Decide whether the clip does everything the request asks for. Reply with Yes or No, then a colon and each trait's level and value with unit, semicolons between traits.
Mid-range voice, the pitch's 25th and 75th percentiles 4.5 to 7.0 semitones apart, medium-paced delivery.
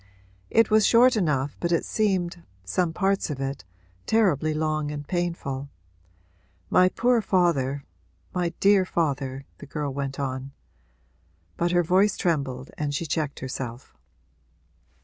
No: medium, 155 Hz; average, 4.8 semitones; slow, 130 wpm